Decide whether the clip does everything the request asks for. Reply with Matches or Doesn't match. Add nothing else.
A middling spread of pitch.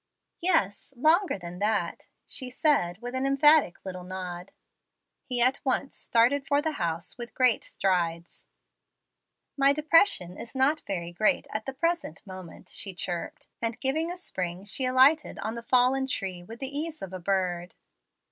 Doesn't match